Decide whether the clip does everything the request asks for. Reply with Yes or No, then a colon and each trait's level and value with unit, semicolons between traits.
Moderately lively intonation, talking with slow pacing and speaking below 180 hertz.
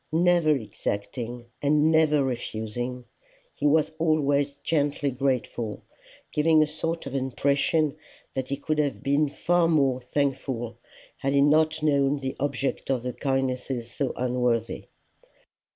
Yes: average, 3.1 semitones; slow, 130 wpm; medium, 140 Hz